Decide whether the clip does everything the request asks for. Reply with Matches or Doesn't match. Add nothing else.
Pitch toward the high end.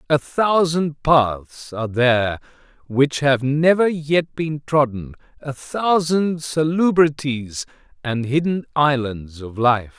Doesn't match